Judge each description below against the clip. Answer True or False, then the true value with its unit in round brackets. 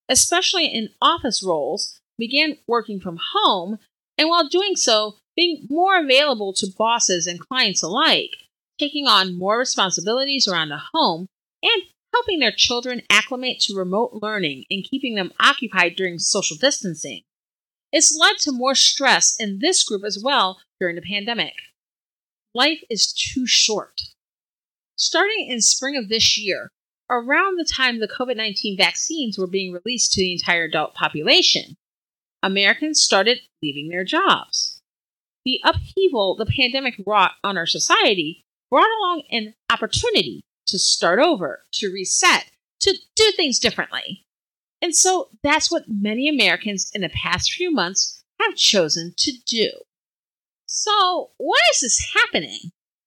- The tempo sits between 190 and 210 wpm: False (140 wpm)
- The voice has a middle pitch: False (240 Hz)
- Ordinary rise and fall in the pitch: False (8.2 semitones)